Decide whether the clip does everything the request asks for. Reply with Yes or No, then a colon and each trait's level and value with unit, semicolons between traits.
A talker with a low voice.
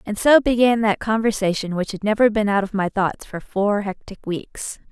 No: high, 210 Hz